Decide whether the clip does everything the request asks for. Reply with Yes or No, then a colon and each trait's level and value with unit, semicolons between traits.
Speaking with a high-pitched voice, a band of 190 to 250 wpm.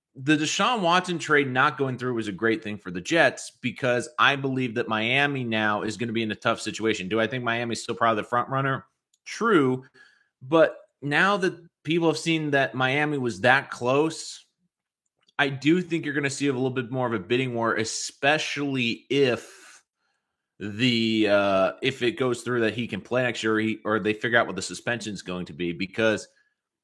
No: low, 125 Hz; fast, 205 wpm